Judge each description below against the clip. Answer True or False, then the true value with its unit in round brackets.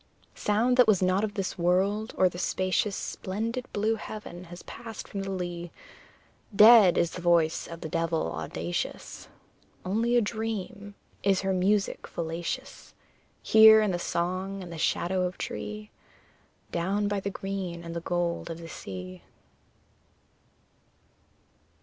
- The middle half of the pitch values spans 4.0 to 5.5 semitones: False (3.3 semitones)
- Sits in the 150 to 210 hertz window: True (185 Hz)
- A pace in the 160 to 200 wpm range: False (145 wpm)